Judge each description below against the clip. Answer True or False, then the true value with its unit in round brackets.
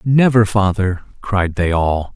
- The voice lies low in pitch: True (100 Hz)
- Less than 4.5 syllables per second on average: True (3.8 syllables/s)